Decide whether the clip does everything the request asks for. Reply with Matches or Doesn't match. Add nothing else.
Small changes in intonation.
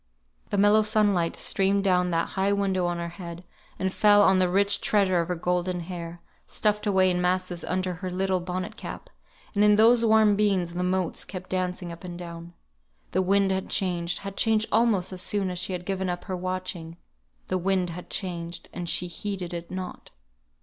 Matches